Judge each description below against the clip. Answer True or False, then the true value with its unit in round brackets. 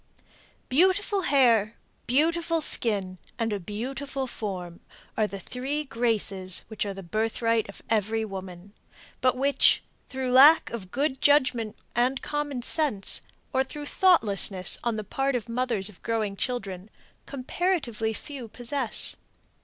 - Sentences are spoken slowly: True (130 wpm)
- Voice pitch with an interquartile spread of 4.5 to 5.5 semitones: True (4.8 semitones)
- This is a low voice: False (235 Hz)